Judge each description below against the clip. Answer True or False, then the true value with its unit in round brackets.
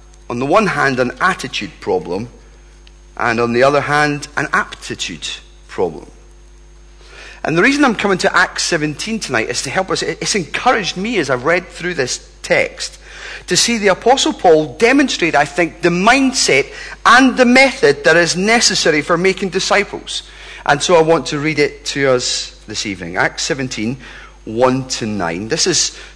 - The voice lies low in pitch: False (175 Hz)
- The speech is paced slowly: False (170 wpm)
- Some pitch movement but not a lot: False (8.6 semitones)